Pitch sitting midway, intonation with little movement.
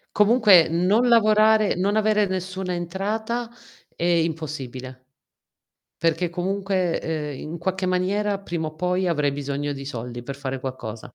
No: medium, 175 Hz; wide, 5.5 semitones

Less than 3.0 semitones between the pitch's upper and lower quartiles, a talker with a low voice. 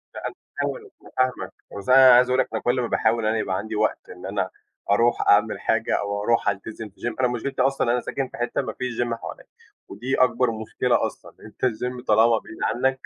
Yes: narrow, 2.5 semitones; low, 120 Hz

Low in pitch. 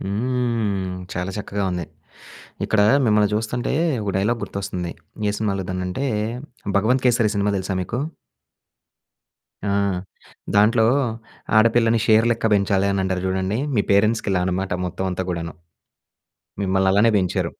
Yes: low, 100 Hz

